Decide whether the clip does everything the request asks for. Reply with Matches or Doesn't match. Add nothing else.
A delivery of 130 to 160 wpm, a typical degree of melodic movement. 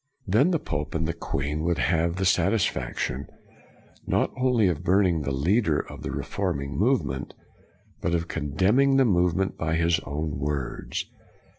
Matches